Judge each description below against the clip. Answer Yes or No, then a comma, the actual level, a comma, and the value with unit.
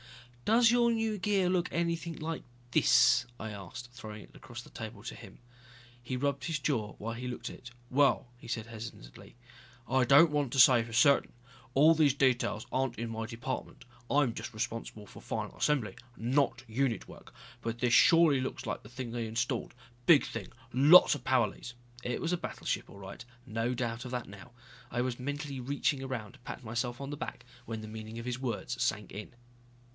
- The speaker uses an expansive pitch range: No, average, 3.8 semitones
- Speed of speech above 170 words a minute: Yes, average, 200 wpm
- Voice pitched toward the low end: Yes, low, 125 Hz